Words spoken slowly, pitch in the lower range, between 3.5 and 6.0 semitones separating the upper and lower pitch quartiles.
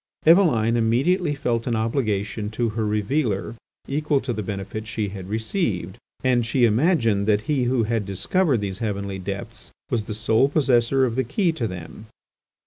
No: average, 165 wpm; low, 115 Hz; average, 4.2 semitones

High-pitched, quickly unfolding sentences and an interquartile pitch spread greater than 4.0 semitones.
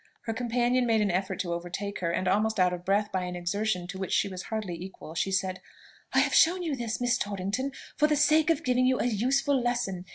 Yes: high, 210 Hz; fast, 235 wpm; average, 5.2 semitones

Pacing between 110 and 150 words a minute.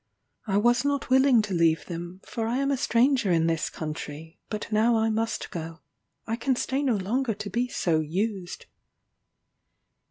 No: average, 170 wpm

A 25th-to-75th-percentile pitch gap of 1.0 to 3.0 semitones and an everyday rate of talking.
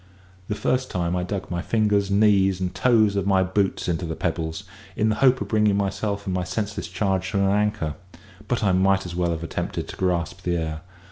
No: average, 2.7 semitones; fast, 220 wpm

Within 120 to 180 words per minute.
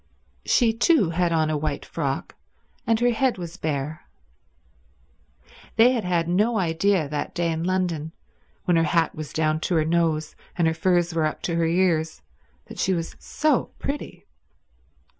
Yes: average, 165 wpm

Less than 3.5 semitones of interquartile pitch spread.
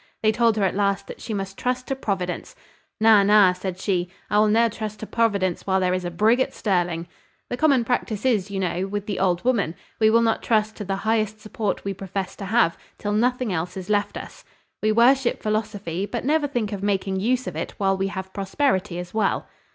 Yes: average, 3.0 semitones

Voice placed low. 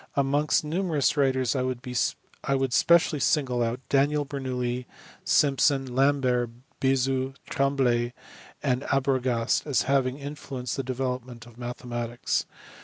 Yes: low, 130 Hz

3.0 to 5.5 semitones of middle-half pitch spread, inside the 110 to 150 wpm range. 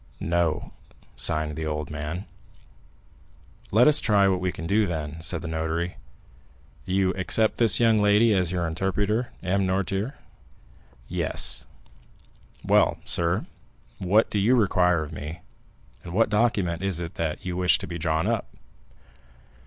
Yes: average, 3.8 semitones; average, 145 wpm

